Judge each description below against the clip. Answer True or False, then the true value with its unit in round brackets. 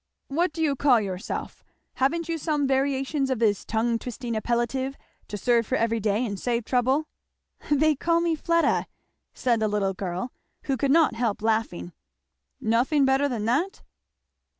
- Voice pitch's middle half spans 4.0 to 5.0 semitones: True (4.3 semitones)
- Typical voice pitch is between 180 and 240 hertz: False (250 Hz)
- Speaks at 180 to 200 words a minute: False (160 wpm)